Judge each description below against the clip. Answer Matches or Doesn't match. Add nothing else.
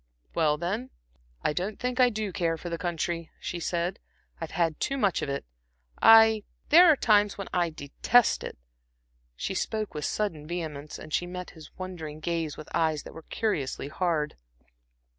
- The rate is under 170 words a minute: Doesn't match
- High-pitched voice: Doesn't match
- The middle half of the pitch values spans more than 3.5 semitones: Matches